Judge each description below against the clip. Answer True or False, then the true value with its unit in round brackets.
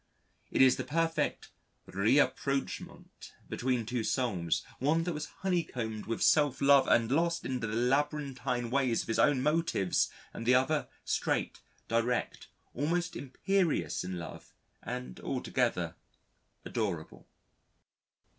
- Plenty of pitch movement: False (4.5 semitones)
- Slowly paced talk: True (120 wpm)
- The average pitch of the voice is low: True (130 Hz)